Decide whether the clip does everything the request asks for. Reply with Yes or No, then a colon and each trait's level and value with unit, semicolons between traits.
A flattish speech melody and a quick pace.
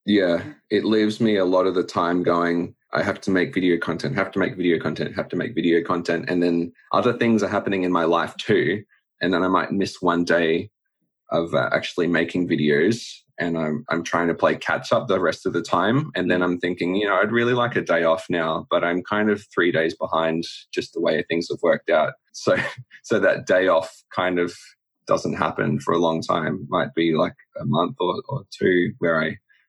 Yes: narrow, 1.7 semitones; fast, 225 wpm